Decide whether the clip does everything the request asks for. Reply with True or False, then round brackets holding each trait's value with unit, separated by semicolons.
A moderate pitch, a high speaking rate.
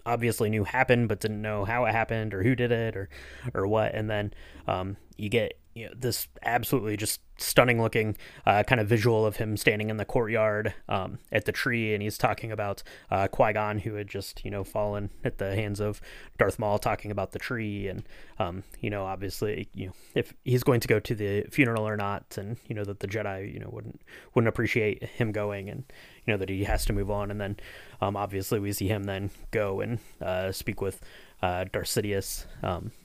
False (105 Hz; 215 wpm)